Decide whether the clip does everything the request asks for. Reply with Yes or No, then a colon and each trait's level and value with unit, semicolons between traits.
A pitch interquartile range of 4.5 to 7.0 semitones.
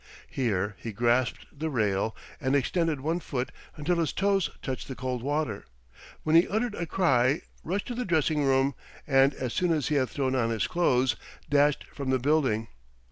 No: average, 4.1 semitones